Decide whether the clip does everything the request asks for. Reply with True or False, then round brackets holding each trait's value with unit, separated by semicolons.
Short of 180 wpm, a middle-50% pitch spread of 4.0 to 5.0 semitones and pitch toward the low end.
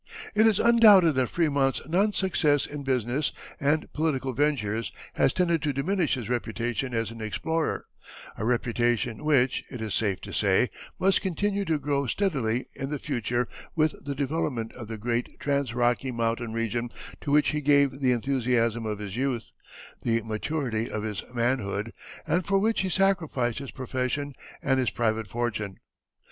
True (165 wpm; 4.6 semitones; 130 Hz)